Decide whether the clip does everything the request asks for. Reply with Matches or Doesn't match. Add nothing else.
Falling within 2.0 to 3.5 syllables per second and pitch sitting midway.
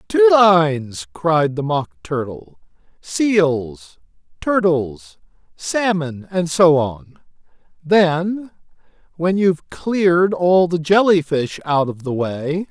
Matches